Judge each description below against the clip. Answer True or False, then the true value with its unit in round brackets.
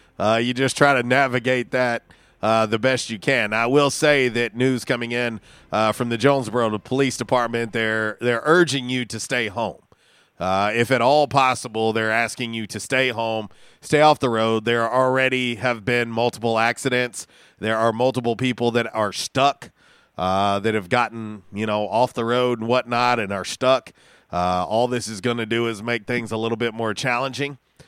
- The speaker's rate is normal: True (190 wpm)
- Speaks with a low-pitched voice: True (120 Hz)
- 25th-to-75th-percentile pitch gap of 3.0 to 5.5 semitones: False (2.4 semitones)